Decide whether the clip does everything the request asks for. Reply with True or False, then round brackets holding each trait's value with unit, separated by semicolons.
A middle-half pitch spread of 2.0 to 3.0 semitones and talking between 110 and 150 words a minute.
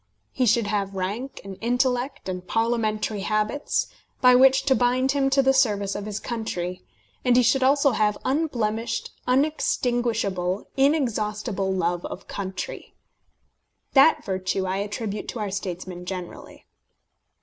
False (4.7 semitones; 135 wpm)